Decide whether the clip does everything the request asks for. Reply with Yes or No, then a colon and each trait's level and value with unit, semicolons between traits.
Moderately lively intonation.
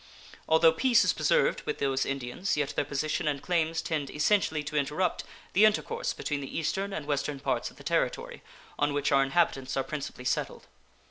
Yes: average, 3.8 semitones